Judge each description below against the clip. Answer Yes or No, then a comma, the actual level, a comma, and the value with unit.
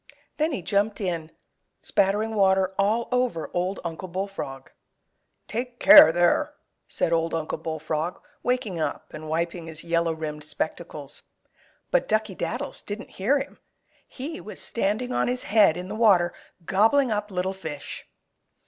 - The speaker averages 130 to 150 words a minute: Yes, average, 145 wpm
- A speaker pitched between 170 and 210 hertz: Yes, high, 190 Hz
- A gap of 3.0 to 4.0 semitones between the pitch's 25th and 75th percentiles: No, average, 5.0 semitones